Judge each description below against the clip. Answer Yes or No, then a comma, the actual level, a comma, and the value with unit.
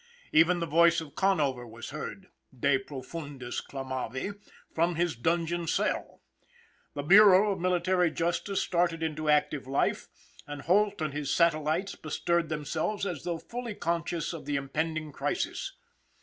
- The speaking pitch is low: No, medium, 165 Hz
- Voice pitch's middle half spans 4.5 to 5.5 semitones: No, average, 3.1 semitones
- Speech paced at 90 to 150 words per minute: Yes, average, 140 wpm